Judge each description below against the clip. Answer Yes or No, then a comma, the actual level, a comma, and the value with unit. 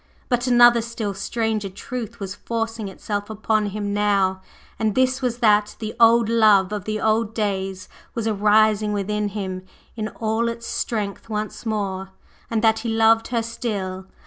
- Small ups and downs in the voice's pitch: Yes, narrow, 2.1 semitones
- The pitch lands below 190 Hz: No, high, 215 Hz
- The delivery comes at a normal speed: Yes, average, 165 wpm